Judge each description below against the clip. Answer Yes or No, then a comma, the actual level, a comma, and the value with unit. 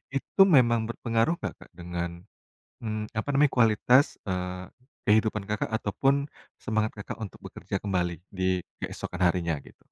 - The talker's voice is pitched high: No, low, 105 Hz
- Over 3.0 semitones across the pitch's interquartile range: Yes, average, 4.3 semitones